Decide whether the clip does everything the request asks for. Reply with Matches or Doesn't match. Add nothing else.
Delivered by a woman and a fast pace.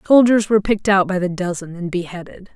Matches